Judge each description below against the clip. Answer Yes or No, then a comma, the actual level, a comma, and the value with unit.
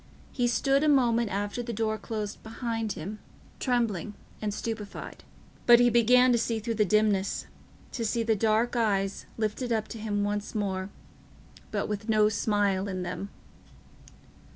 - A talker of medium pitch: No, high, 220 Hz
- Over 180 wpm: No, average, 155 wpm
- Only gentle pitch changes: Yes, narrow, 2.3 semitones